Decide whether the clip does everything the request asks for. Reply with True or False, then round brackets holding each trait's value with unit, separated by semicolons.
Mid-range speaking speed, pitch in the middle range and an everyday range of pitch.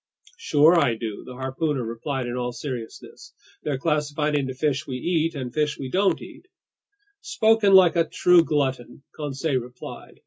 True (160 wpm; 145 Hz; 4.1 semitones)